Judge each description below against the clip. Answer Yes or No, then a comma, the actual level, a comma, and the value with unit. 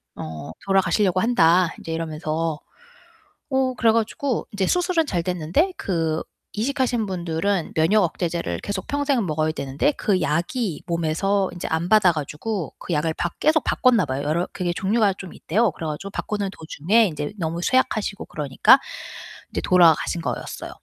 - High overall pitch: No, medium, 180 Hz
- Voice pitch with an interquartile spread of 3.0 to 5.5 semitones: Yes, average, 5.1 semitones